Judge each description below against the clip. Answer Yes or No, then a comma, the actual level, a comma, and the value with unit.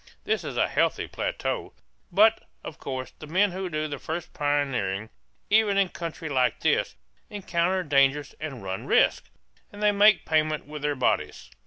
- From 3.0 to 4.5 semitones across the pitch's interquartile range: No, average, 5.1 semitones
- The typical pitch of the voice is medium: Yes, medium, 155 Hz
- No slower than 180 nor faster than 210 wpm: No, average, 165 wpm